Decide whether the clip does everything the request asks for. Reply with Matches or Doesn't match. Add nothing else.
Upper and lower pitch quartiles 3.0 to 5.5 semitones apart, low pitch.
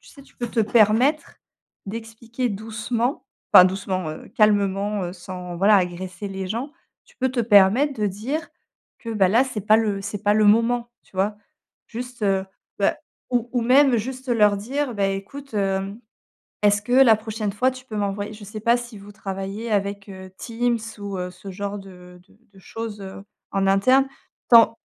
Doesn't match